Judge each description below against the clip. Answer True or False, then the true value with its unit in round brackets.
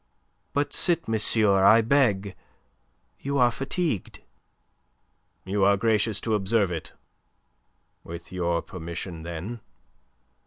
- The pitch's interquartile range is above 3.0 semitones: True (4.2 semitones)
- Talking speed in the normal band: False (105 wpm)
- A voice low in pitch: True (105 Hz)